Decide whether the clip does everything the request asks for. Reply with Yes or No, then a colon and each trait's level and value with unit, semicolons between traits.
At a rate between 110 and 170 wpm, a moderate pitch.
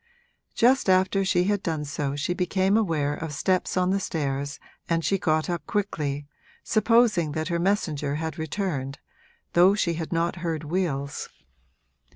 Yes: average, 155 wpm; medium, 170 Hz